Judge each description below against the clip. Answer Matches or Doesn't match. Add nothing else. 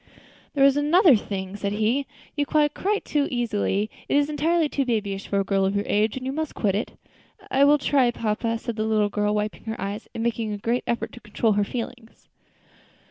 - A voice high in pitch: Matches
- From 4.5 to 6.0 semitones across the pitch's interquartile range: Matches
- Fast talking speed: Matches